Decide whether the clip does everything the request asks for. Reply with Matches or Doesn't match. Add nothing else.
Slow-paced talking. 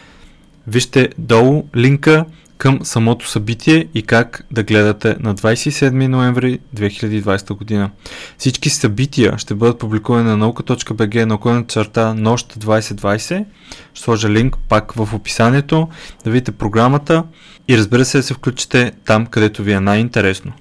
Doesn't match